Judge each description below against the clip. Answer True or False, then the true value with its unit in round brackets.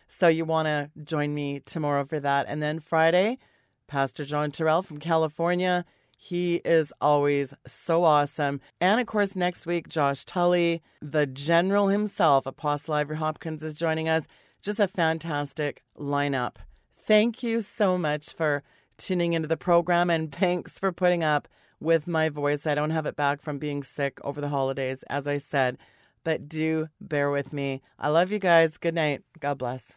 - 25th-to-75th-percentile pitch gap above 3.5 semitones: False (2.9 semitones)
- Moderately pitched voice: True (155 Hz)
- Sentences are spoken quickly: False (170 wpm)